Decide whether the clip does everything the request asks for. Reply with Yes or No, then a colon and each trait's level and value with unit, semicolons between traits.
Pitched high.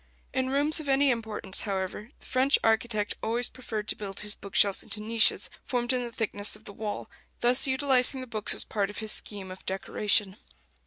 Yes: high, 220 Hz